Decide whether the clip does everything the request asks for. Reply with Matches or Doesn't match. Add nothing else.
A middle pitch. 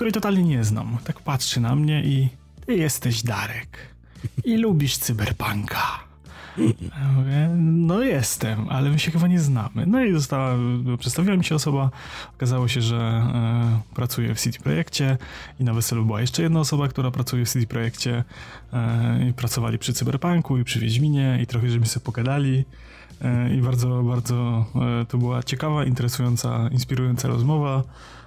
Doesn't match